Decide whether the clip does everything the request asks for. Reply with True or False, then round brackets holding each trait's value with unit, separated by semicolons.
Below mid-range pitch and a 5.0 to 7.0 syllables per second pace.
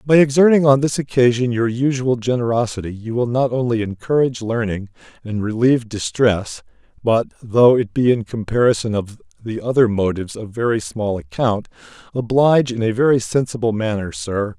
False (120 Hz; 4.5 syllables/s)